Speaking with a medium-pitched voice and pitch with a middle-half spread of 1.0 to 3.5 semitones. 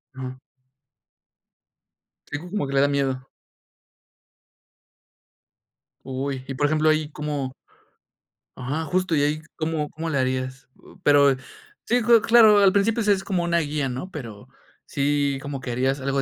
No: medium, 145 Hz; average, 4.0 semitones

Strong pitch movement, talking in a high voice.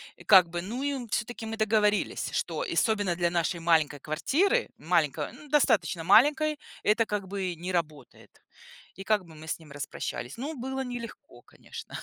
Yes: wide, 6.1 semitones; high, 205 Hz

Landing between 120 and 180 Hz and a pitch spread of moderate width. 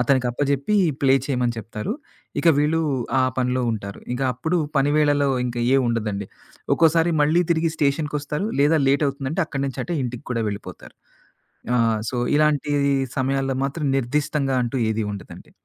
Yes: medium, 140 Hz; average, 3.3 semitones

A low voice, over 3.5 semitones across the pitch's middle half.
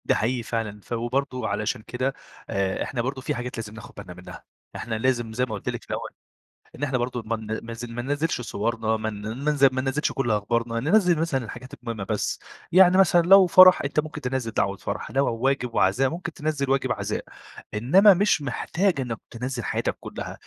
Yes: low, 125 Hz; average, 4.0 semitones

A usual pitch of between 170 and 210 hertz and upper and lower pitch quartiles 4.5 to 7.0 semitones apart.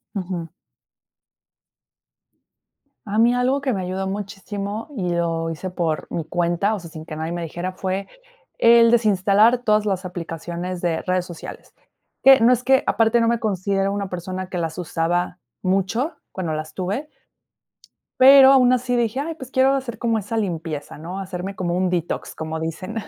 Yes: high, 190 Hz; average, 4.8 semitones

